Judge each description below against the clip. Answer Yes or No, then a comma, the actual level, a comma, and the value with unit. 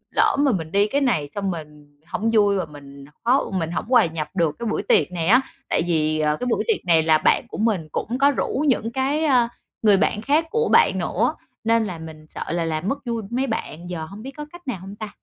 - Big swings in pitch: Yes, wide, 7.3 semitones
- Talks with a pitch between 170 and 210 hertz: Yes, high, 200 Hz